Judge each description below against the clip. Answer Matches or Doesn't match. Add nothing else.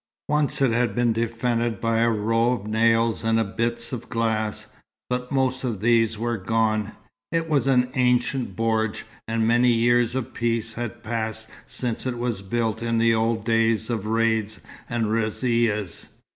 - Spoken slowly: Doesn't match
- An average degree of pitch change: Doesn't match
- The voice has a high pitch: Doesn't match